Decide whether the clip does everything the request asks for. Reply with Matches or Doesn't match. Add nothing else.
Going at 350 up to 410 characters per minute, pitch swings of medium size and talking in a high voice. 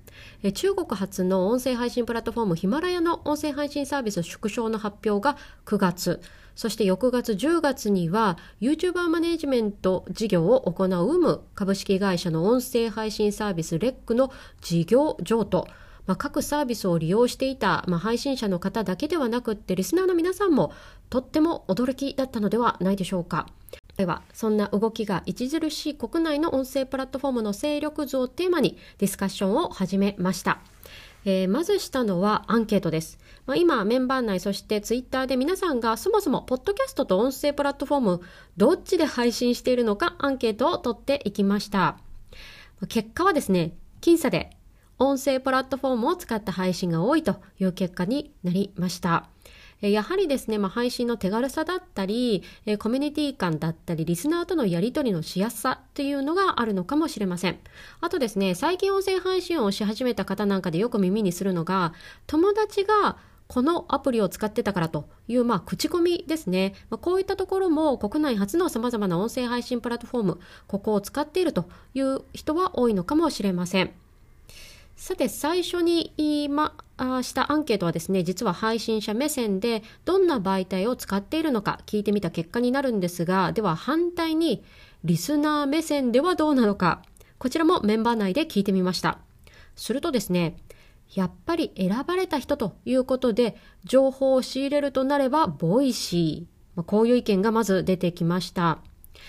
Doesn't match